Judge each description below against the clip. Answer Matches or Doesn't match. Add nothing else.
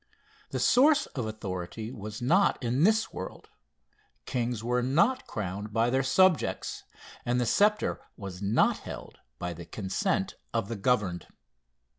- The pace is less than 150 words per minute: Matches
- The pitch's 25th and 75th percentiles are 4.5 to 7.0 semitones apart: Matches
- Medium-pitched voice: Doesn't match